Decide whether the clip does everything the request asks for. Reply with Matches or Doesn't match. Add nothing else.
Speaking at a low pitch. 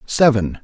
Matches